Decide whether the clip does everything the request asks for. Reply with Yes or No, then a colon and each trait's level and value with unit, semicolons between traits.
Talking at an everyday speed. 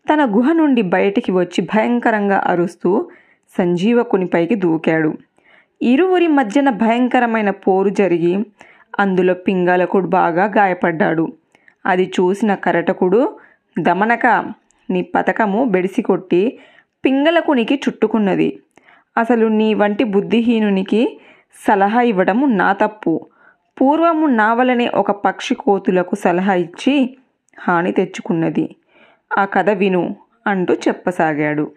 Yes: average, 95 wpm